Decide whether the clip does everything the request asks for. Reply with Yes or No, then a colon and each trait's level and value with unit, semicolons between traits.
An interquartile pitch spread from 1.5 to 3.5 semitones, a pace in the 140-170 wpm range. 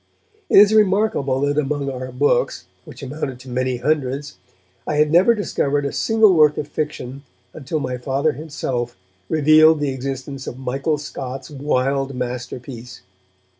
Yes: average, 3.0 semitones; average, 145 wpm